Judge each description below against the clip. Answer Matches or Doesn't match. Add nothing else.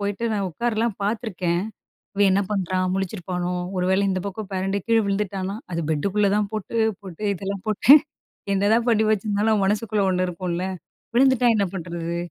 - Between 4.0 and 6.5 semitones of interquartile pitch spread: Doesn't match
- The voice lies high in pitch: Matches